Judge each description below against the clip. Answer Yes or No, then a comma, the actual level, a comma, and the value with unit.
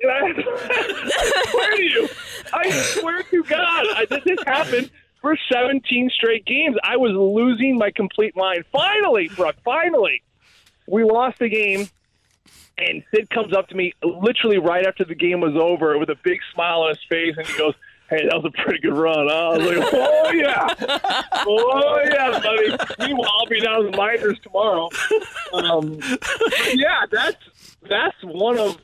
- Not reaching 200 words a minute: Yes, average, 170 wpm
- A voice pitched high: Yes, high, 225 Hz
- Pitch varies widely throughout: Yes, wide, 8.1 semitones